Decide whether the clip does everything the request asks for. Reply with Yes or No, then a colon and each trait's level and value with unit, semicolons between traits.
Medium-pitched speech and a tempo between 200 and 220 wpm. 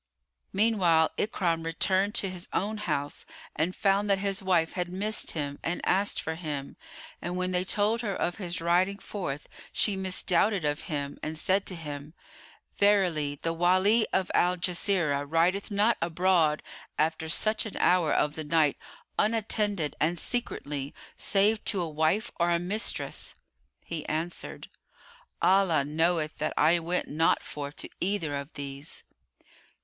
No: medium, 175 Hz; average, 150 wpm